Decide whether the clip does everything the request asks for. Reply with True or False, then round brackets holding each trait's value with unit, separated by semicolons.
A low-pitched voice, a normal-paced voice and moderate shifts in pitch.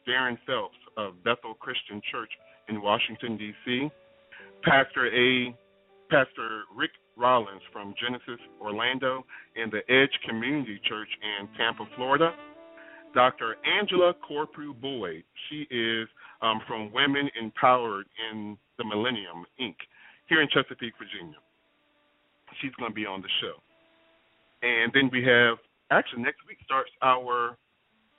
False (125 Hz; 125 wpm; 3.9 semitones)